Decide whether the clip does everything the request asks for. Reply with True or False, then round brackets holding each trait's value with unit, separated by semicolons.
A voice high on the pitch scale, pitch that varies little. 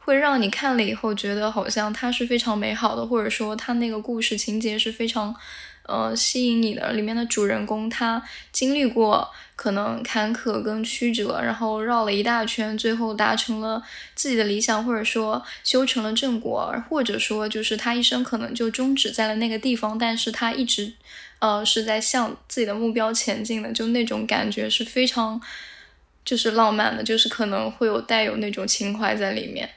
True (225 Hz; 1.7 semitones)